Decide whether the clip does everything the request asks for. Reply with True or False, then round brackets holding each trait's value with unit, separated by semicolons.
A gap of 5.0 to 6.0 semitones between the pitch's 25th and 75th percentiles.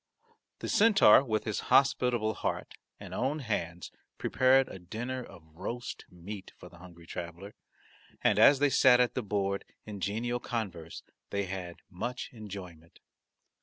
True (5.6 semitones)